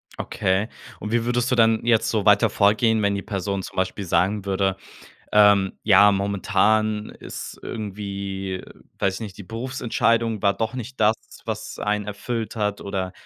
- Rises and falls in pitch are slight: Yes, narrow, 2.2 semitones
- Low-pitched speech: Yes, low, 105 Hz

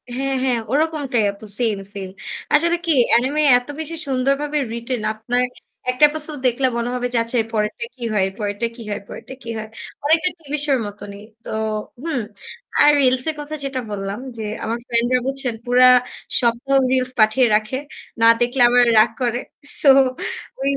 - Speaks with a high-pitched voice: Yes, very high, 250 Hz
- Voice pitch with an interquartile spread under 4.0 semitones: Yes, average, 3.4 semitones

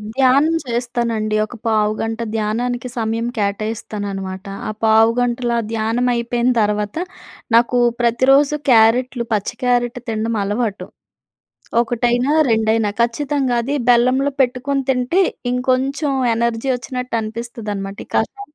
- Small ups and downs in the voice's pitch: Yes, narrow, 2.3 semitones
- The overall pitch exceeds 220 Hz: Yes, high, 235 Hz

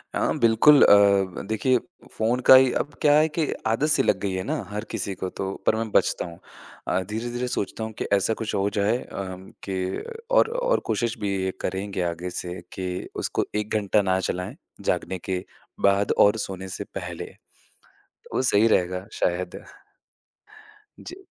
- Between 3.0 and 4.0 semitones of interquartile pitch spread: Yes, average, 3.6 semitones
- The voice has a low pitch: Yes, low, 100 Hz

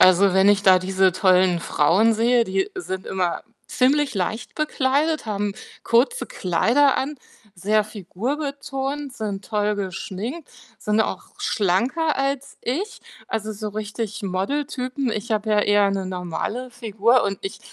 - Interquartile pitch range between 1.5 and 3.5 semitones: No, wide, 5.6 semitones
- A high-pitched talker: Yes, high, 215 Hz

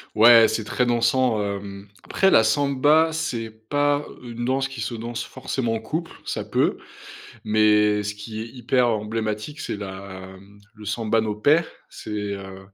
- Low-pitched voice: Yes, low, 110 Hz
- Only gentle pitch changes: No, average, 3.3 semitones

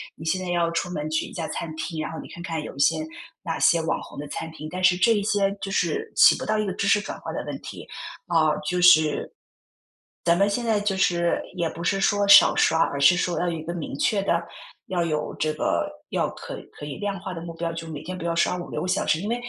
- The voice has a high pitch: No, medium, 175 Hz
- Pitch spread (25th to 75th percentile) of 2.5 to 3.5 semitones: Yes, average, 3.2 semitones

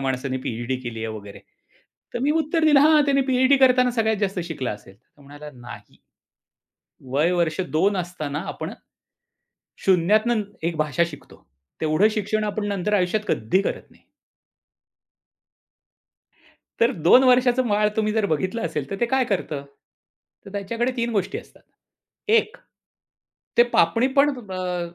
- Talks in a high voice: Yes, high, 200 Hz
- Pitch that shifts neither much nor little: No, wide, 7.5 semitones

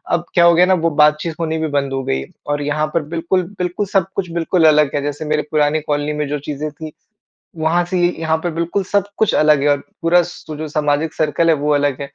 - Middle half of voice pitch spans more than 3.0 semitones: No, narrow, 2.6 semitones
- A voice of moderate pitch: Yes, medium, 155 Hz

